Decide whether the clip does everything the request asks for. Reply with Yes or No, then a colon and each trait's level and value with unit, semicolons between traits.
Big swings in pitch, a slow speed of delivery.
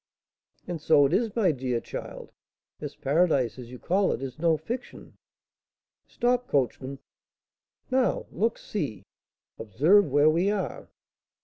Yes: wide, 7.4 semitones; slow, 130 wpm